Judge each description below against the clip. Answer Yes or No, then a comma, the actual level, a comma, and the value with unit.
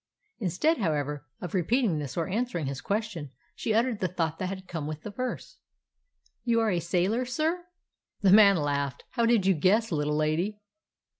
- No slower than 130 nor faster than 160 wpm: No, average, 180 wpm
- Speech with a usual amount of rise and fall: No, wide, 6.4 semitones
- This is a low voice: No, medium, 185 Hz